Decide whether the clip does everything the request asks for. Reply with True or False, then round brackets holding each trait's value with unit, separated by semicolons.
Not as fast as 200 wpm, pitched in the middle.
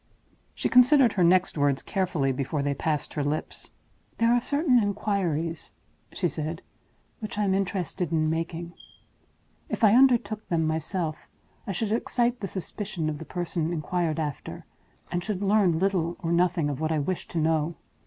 True (165 wpm; 175 Hz)